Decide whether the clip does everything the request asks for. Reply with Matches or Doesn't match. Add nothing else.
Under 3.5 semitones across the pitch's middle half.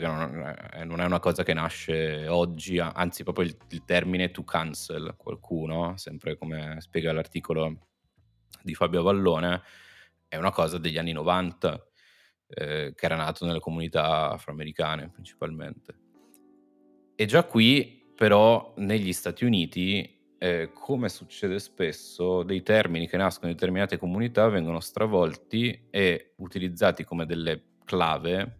Matches